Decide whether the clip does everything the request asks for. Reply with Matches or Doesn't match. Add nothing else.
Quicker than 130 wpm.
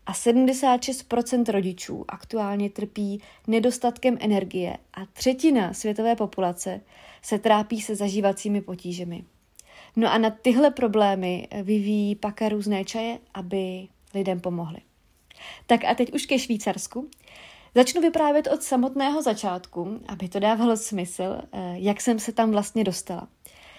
Doesn't match